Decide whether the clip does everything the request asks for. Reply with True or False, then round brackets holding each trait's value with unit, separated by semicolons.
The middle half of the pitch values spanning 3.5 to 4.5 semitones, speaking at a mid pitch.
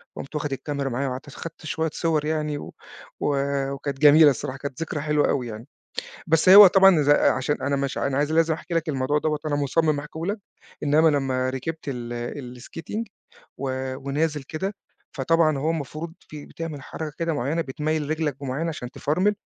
False (2.8 semitones; 150 Hz)